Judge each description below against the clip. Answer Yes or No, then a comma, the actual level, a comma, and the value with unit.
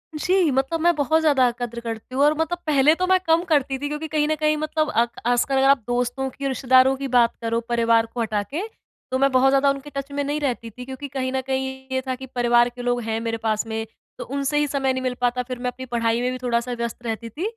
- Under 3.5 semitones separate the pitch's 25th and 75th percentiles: Yes, average, 3.1 semitones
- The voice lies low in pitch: No, very high, 260 Hz